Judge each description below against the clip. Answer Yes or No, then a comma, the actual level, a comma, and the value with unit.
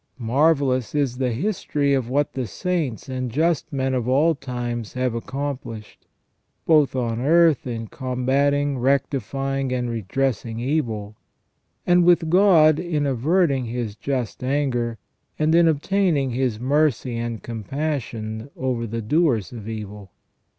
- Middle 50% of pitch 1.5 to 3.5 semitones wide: No, average, 3.9 semitones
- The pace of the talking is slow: Yes, slow, 130 wpm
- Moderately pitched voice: No, low, 130 Hz